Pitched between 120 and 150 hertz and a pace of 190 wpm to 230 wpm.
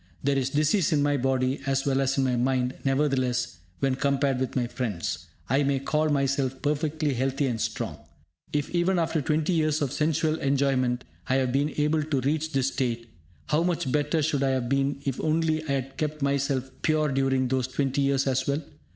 Yes: medium, 140 Hz; average, 195 wpm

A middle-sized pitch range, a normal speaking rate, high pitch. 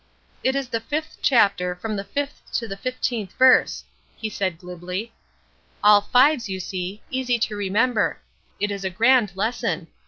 Yes: average, 4.6 semitones; average, 160 wpm; high, 215 Hz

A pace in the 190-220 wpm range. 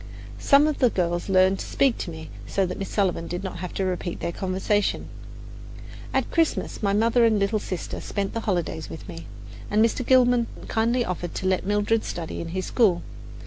Yes: average, 195 wpm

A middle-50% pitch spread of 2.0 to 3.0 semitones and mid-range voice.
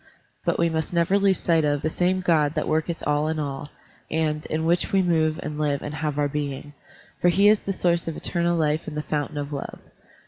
Yes: narrow, 2.5 semitones; medium, 155 Hz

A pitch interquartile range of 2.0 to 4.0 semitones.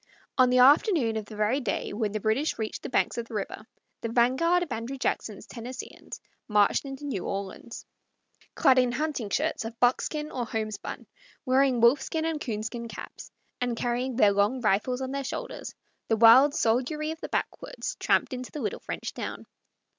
Yes: average, 3.5 semitones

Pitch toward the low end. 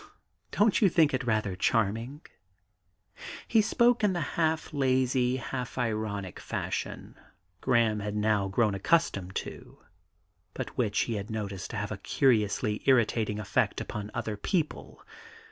Yes: low, 115 Hz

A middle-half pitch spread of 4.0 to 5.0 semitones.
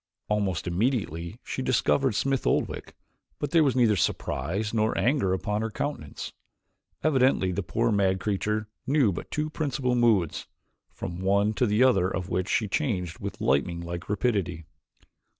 No: wide, 5.6 semitones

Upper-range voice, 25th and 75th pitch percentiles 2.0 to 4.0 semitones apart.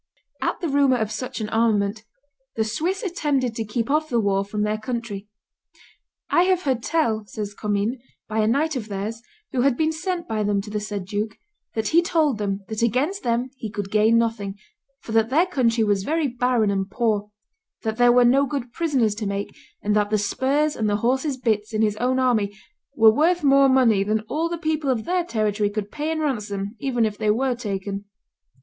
No: high, 230 Hz; average, 4.6 semitones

